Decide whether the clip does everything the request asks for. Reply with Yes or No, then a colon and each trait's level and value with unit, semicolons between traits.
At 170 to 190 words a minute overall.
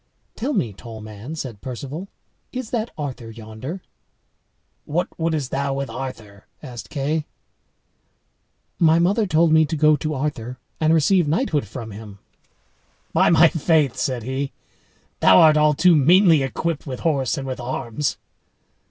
No: average, 145 wpm